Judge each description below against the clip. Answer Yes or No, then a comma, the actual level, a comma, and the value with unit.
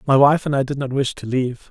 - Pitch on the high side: No, low, 135 Hz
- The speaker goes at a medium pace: No, fast, 315 wpm